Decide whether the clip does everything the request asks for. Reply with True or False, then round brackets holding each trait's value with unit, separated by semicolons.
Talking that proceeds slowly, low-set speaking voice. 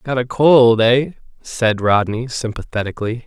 True (130 wpm; 120 Hz)